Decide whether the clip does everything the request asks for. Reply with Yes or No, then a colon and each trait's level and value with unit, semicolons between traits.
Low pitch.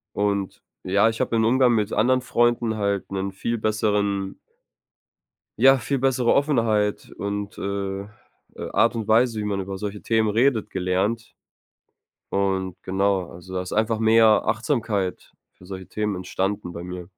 Yes: low, 105 Hz